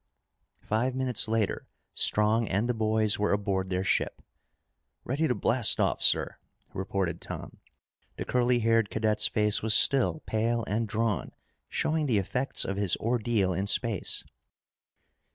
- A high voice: No, low, 110 Hz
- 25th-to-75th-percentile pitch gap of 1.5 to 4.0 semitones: Yes, average, 2.9 semitones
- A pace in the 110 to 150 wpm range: Yes, average, 140 wpm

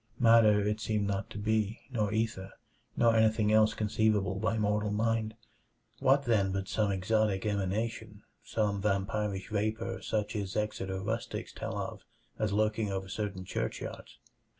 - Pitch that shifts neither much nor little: No, narrow, 1.6 semitones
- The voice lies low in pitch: Yes, low, 105 Hz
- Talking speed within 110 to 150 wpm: Yes, average, 145 wpm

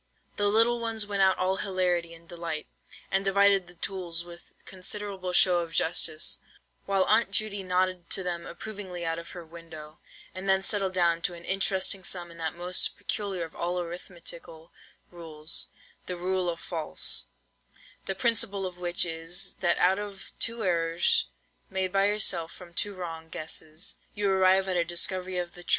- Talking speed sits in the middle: Yes, average, 170 wpm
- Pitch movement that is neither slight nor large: No, narrow, 2.3 semitones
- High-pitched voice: No, medium, 180 Hz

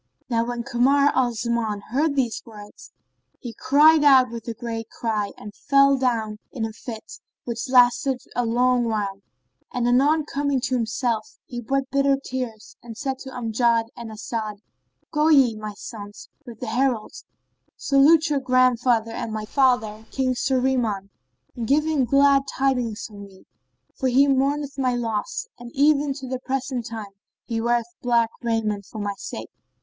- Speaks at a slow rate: No, average, 170 wpm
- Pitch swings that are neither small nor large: Yes, average, 3.3 semitones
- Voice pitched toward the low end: No, high, 245 Hz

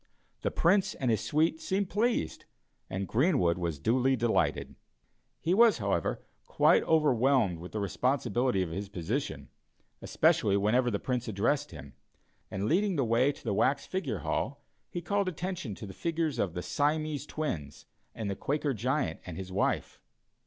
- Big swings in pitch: Yes, wide, 7.7 semitones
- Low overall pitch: Yes, low, 125 Hz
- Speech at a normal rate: Yes, average, 160 wpm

